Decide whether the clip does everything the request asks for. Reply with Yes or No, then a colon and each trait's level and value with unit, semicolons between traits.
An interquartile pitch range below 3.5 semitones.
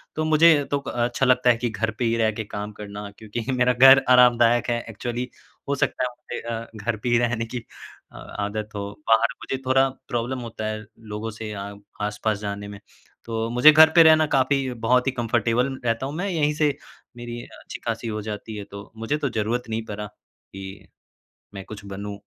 Yes: average, 2.9 semitones